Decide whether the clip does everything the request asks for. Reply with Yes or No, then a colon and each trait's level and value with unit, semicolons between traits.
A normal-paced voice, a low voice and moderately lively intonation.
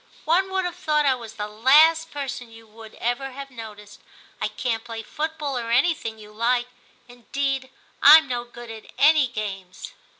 No: average, 175 wpm; high, 245 Hz; average, 4.4 semitones